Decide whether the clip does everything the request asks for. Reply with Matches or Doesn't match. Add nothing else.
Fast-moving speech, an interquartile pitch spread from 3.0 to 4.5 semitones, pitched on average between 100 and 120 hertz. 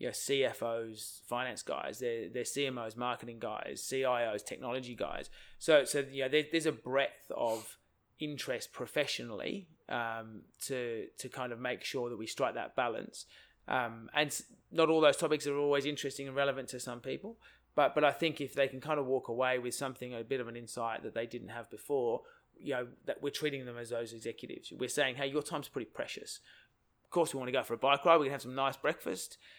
Doesn't match